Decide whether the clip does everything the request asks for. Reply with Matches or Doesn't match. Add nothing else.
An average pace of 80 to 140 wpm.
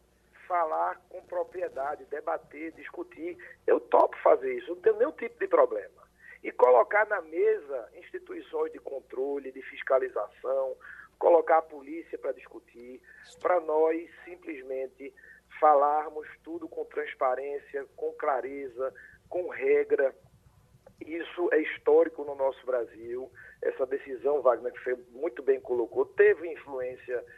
Matches